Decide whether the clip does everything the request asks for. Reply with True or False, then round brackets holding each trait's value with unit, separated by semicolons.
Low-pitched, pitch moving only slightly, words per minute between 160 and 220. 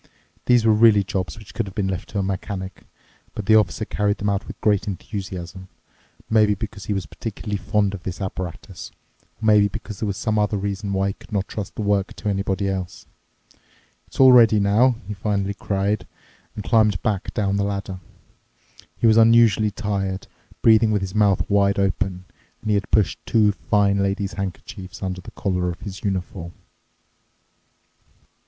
True (100 Hz; 1.8 semitones; 180 wpm)